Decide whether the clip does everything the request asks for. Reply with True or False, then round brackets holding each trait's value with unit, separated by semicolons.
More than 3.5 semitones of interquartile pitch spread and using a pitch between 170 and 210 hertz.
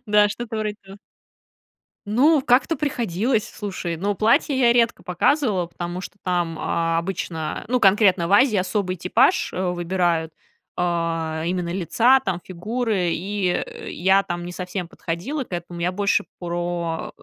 True (3.9 semitones; 185 Hz)